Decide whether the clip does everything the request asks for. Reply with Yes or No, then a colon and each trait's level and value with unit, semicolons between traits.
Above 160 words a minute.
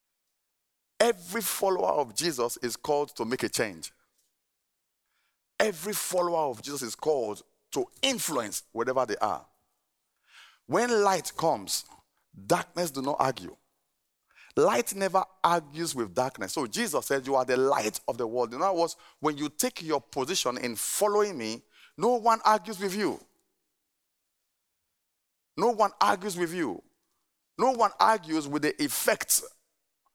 No: average, 140 wpm